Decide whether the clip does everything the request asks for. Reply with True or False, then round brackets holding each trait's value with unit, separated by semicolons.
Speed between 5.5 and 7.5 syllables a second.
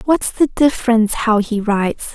False (5.0 syllables/s)